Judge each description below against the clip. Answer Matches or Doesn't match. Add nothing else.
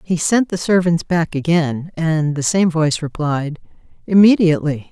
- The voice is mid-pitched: Matches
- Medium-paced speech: Matches